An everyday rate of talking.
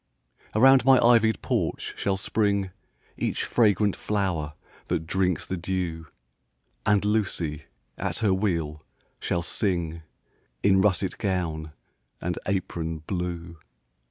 No: slow, 110 wpm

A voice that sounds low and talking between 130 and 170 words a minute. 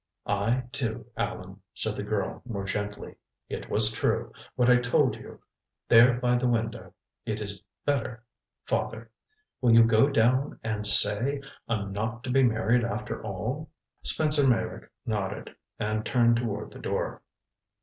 Yes: low, 115 Hz; average, 150 wpm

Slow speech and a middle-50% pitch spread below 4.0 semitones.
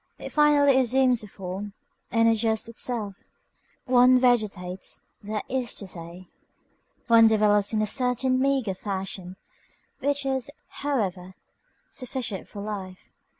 No: slow, 120 wpm; average, 4.5 semitones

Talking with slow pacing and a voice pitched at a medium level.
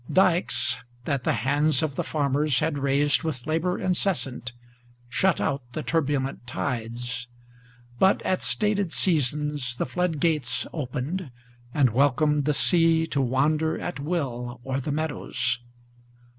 Yes: slow, 130 wpm; medium, 145 Hz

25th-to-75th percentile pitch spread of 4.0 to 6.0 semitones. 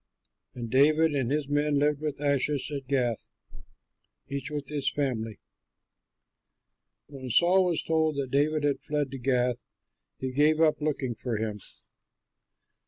No: narrow, 2.6 semitones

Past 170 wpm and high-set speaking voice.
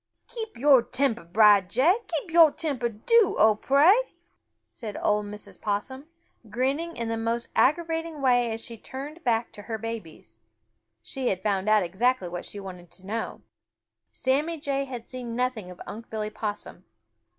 No: average, 160 wpm; high, 235 Hz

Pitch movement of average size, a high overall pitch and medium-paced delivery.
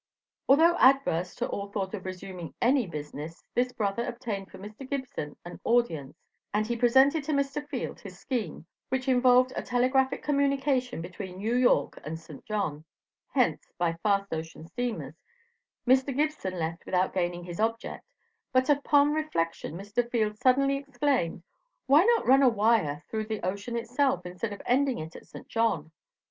No: wide, 6.4 semitones; high, 230 Hz; average, 160 wpm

